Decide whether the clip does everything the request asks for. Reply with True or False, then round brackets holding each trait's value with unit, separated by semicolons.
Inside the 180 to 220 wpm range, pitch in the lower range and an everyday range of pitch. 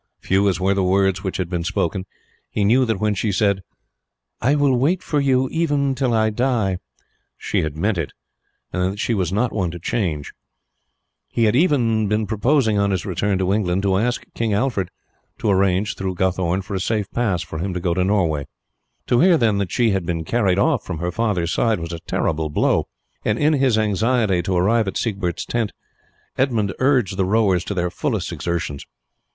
True (200 wpm; 100 Hz; 4.2 semitones)